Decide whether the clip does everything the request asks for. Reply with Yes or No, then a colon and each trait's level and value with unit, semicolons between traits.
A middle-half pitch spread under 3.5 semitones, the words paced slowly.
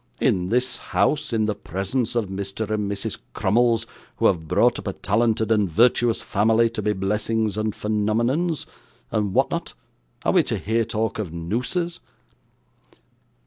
No: narrow, 2.6 semitones; average, 155 wpm